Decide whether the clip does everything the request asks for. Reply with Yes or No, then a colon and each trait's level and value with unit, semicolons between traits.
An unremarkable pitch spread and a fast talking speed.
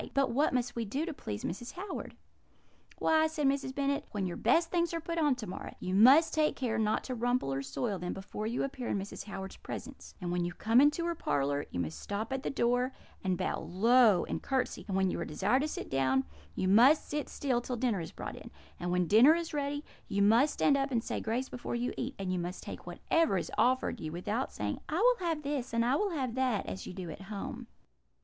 No: wide, 6.6 semitones; fast, 240 wpm